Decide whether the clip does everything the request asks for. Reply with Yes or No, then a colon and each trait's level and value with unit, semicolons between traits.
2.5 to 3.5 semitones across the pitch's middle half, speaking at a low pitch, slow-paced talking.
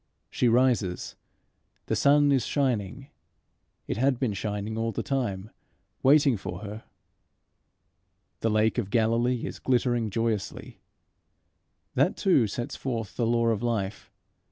Yes: average, 3.1 semitones; low, 115 Hz; slow, 130 wpm